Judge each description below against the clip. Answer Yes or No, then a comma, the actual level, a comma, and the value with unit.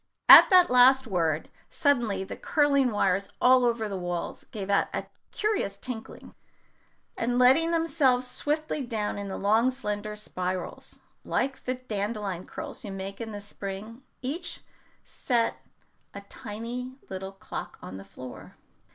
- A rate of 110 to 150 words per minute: Yes, average, 140 wpm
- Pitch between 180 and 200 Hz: No, high, 225 Hz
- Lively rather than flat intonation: No, average, 4.6 semitones